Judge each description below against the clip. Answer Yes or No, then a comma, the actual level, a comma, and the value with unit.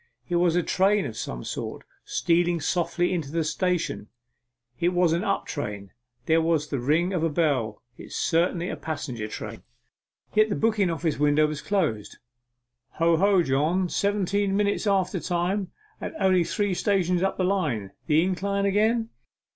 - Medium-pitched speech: Yes, medium, 175 Hz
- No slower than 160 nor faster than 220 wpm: Yes, average, 170 wpm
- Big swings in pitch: No, average, 4.0 semitones